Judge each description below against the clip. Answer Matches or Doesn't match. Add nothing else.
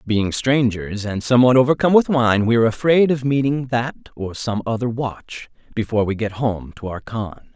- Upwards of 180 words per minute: Matches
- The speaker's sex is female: Doesn't match